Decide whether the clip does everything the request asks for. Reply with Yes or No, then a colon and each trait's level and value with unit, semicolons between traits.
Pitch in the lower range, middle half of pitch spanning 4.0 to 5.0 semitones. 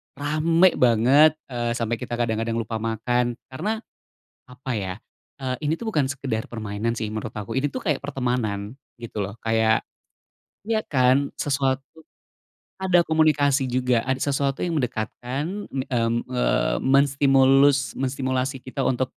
No: low, 130 Hz; average, 3.5 semitones